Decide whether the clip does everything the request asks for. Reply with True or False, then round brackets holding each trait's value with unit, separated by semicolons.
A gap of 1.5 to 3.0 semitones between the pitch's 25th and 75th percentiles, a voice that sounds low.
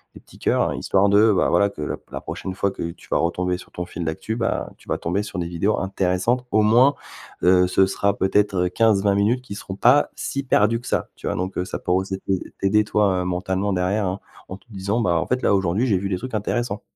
True (2.7 semitones; 100 Hz)